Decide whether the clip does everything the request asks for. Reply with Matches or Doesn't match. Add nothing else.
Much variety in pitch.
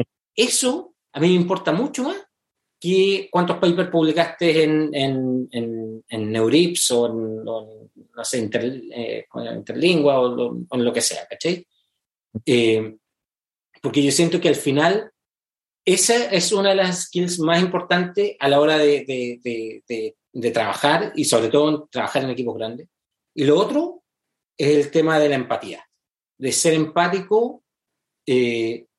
Matches